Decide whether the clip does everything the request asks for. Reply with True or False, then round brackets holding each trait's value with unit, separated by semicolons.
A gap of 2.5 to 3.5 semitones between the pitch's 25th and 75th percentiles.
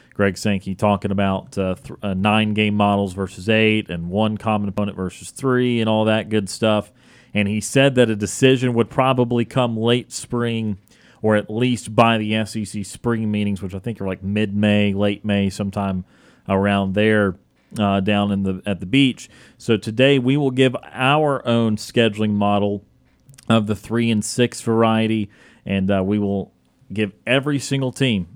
True (2.8 semitones)